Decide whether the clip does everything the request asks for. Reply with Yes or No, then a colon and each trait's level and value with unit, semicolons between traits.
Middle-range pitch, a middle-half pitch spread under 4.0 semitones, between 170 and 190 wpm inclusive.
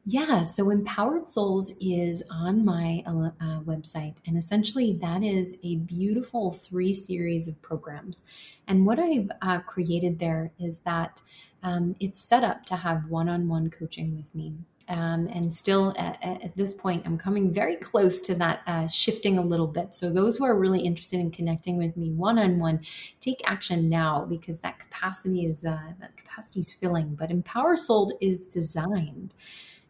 Yes: medium, 175 Hz; average, 2.7 semitones; average, 175 wpm